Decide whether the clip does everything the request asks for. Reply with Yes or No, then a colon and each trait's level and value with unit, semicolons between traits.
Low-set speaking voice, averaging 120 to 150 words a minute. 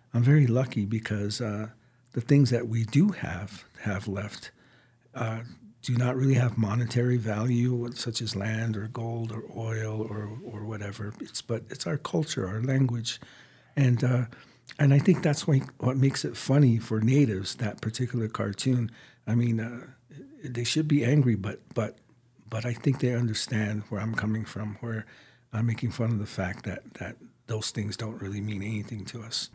No: low, 115 Hz; average, 175 wpm